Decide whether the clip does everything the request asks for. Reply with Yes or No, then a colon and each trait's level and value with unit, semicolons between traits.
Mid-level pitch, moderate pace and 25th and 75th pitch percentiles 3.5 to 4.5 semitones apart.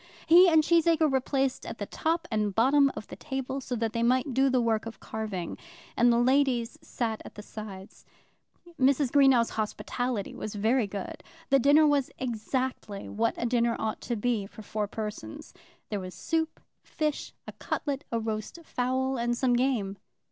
No: high, 245 Hz; average, 175 wpm; average, 3.8 semitones